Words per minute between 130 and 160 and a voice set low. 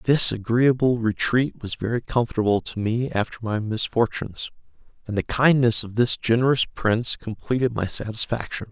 Yes: average, 145 wpm; low, 115 Hz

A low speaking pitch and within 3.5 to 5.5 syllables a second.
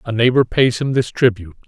No: low, 115 Hz; 6.0 syllables/s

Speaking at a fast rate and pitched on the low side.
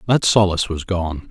No: average, 185 wpm; very low, 95 Hz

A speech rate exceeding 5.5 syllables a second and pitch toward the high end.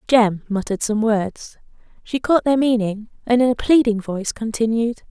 No: 5.0 syllables/s; high, 225 Hz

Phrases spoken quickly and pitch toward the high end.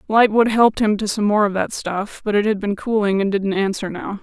Yes: fast, 255 wpm; high, 205 Hz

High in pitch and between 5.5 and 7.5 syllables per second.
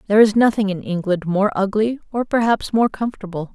Yes: high, 210 Hz; 6.0 syllables/s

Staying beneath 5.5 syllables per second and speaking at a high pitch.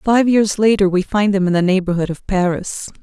Yes: 5.2 syllables/s; high, 195 Hz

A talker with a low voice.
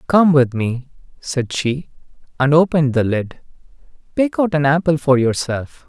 No: medium, 145 Hz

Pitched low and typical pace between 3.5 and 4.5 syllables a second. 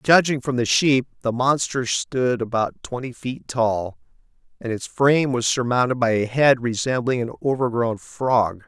Yes: low, 125 Hz; 4.4 syllables/s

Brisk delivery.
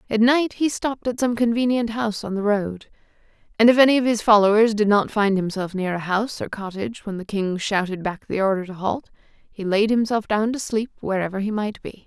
Yes: fast, 225 wpm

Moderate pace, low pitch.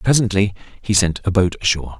Yes: average, 180 wpm; low, 100 Hz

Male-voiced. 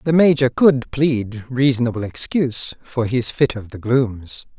Yes: male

